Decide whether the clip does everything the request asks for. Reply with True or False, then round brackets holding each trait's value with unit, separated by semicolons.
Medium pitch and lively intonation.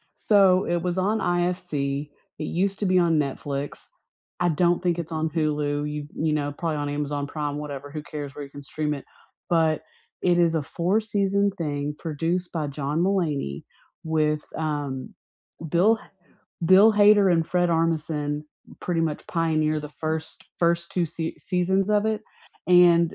False (160 Hz; 3.2 semitones)